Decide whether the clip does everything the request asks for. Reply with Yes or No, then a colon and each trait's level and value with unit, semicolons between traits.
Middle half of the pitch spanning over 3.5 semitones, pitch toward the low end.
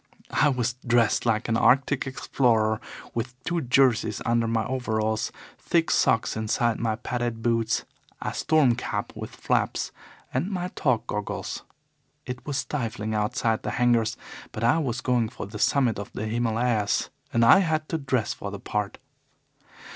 No: average, 2.9 semitones; low, 120 Hz